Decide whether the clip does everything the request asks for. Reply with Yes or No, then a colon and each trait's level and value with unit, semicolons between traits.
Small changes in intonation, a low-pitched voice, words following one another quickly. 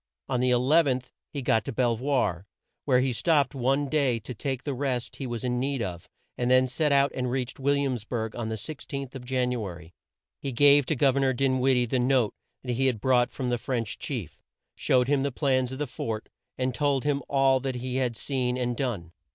Yes: narrow, 2.0 semitones; low, 130 Hz; fast, 230 wpm